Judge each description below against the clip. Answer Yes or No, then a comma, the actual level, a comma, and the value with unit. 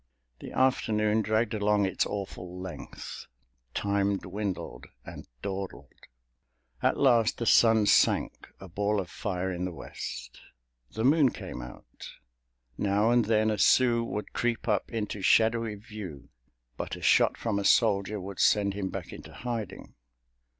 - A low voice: Yes, low, 105 Hz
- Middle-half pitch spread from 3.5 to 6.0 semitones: No, narrow, 2.6 semitones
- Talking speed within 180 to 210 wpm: No, average, 145 wpm